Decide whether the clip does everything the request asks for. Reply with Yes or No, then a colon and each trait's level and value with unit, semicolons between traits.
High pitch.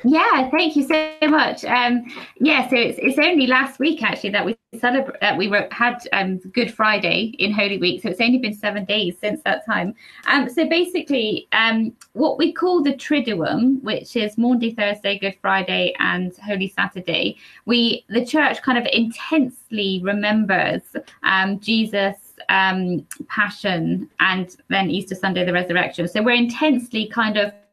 Yes: high, 225 Hz